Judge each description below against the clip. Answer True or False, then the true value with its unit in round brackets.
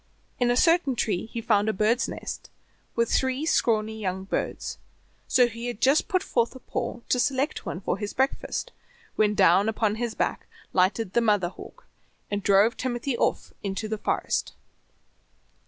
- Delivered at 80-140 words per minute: False (170 wpm)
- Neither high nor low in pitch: False (225 Hz)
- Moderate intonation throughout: True (3.2 semitones)